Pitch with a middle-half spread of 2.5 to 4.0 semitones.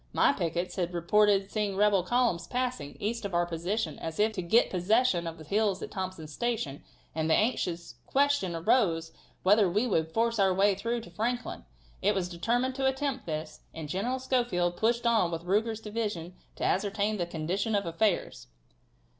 No: average, 4.9 semitones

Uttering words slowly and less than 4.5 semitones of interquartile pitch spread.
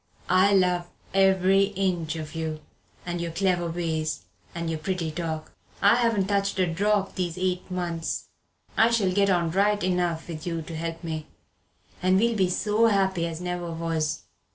No: average, 170 wpm; average, 2.8 semitones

